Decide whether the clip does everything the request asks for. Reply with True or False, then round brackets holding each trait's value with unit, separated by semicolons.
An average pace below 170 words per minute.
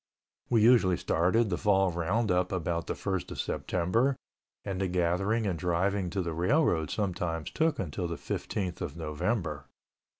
True (155 wpm)